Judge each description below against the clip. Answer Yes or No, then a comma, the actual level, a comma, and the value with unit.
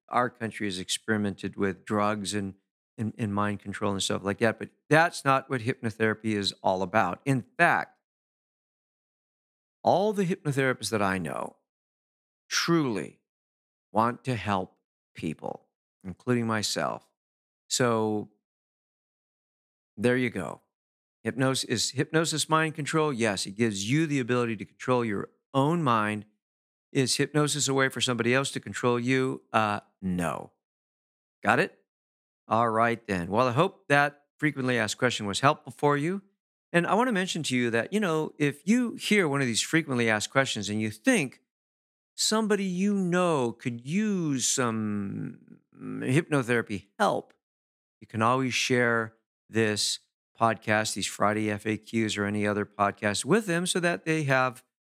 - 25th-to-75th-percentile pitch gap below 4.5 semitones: No, wide, 5.6 semitones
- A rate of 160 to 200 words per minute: No, average, 150 wpm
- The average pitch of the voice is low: Yes, low, 115 Hz